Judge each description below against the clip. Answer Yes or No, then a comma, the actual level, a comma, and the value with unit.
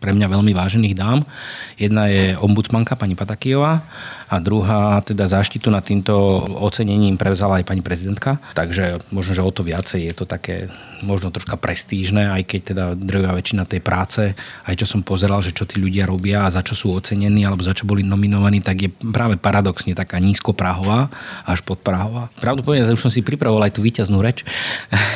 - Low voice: Yes, low, 100 Hz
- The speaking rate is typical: No, fast, 185 wpm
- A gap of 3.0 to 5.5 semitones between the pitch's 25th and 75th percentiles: No, narrow, 2.5 semitones